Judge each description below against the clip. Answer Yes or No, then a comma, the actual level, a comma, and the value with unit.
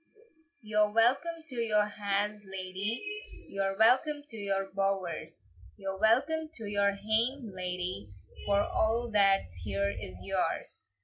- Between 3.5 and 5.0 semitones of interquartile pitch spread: No, average, 2.8 semitones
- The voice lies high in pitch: Yes, high, 205 Hz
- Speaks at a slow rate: Yes, slow, 125 wpm